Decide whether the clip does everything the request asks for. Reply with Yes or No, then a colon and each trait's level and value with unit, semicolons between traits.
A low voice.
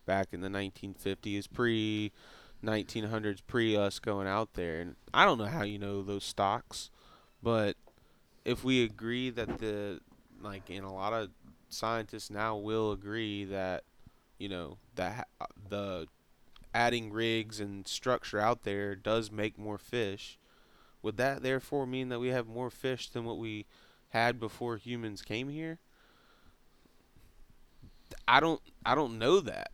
Yes: low, 110 Hz